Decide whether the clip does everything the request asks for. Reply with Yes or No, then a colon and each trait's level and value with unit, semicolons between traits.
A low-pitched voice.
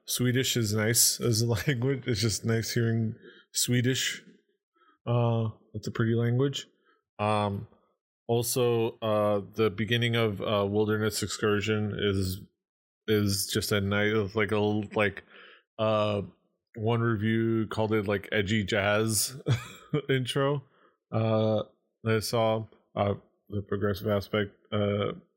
Yes: low, 110 Hz